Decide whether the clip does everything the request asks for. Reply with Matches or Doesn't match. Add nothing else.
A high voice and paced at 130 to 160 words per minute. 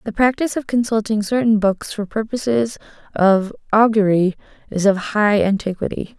Matches